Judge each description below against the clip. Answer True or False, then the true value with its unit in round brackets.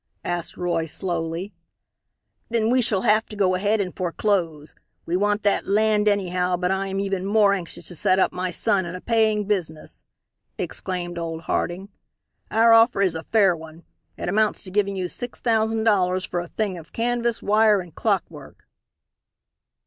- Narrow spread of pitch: False (3.3 semitones)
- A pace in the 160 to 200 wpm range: True (170 wpm)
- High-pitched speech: True (195 Hz)